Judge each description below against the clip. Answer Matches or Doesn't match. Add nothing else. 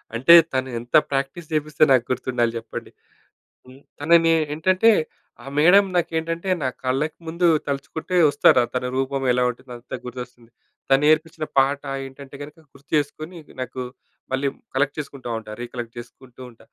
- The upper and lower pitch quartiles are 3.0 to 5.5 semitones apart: Matches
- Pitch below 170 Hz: Matches